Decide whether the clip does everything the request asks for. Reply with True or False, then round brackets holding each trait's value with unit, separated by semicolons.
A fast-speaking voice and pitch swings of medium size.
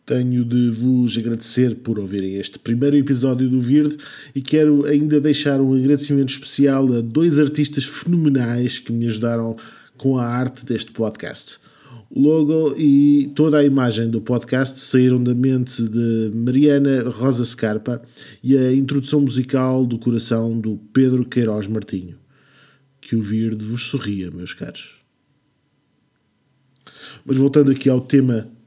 False (140 wpm; 3.2 semitones)